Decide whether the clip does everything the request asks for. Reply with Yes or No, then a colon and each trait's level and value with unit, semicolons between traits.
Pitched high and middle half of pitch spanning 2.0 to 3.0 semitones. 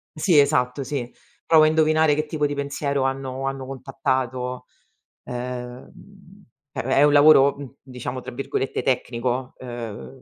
No: low, 135 Hz; narrow, 2.6 semitones